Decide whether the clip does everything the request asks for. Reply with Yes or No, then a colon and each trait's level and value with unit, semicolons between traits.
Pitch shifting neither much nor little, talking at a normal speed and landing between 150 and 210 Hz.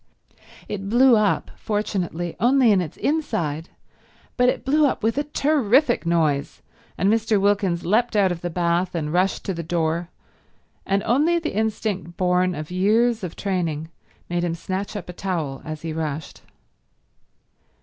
Yes: average, 4.7 semitones; average, 160 wpm; high, 190 Hz